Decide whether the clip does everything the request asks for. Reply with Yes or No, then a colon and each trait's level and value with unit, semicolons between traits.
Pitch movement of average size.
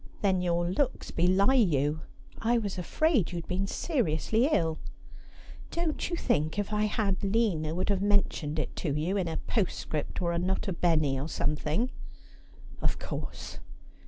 Yes: average, 4.9 semitones